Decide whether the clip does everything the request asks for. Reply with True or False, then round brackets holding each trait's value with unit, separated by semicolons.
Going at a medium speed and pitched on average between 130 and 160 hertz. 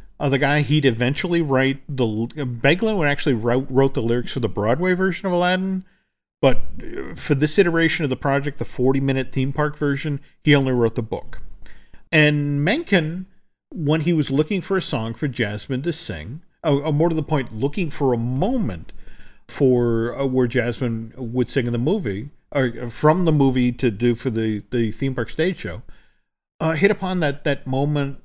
True (190 wpm; 140 Hz)